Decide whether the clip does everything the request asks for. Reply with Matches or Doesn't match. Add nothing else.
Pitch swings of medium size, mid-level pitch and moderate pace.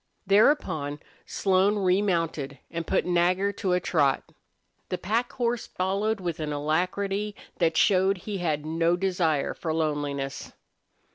Doesn't match